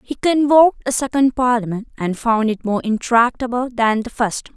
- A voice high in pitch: Yes, high, 240 Hz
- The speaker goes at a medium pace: Yes, average, 170 wpm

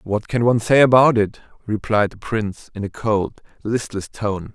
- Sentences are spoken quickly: No, average, 185 wpm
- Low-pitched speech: Yes, low, 110 Hz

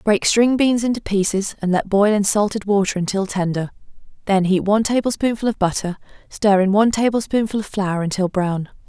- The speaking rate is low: No, average, 180 wpm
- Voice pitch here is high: Yes, high, 205 Hz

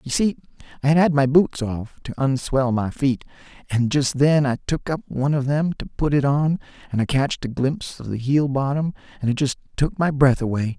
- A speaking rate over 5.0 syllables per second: Yes, 5.3 syllables/s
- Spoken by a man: Yes, male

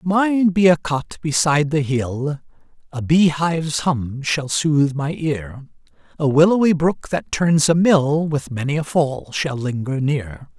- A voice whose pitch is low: No, medium, 150 Hz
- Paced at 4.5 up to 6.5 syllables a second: No, 3.9 syllables/s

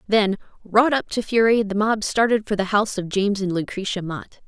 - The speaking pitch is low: No, high, 205 Hz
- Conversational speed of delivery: No, fast, 215 wpm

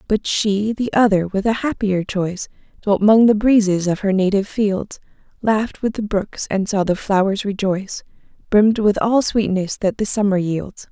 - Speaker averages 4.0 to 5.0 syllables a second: Yes, 4.9 syllables/s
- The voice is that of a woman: Yes, female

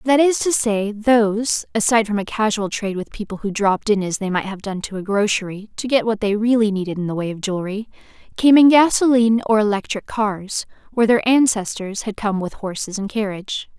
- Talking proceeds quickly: Yes, fast, 215 wpm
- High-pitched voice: Yes, high, 210 Hz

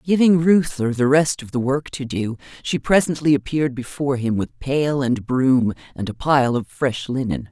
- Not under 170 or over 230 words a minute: Yes, average, 190 wpm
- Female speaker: Yes, female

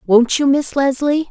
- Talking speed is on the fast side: No, average, 185 wpm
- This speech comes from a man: No, female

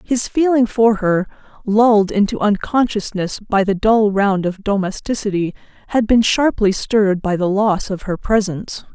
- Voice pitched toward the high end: Yes, high, 210 Hz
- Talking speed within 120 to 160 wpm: Yes, average, 155 wpm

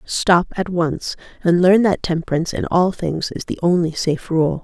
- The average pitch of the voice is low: No, medium, 175 Hz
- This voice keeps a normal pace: Yes, average, 195 wpm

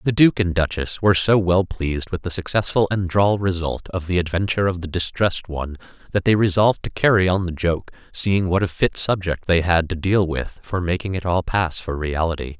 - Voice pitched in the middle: No, very low, 90 Hz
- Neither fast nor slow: No, fast, 220 wpm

